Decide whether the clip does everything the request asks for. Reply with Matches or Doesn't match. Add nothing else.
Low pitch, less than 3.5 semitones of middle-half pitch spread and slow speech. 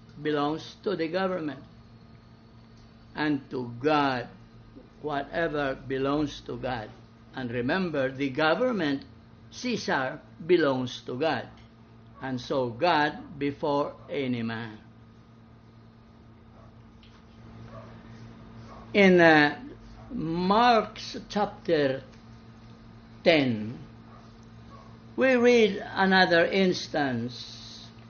Doesn't match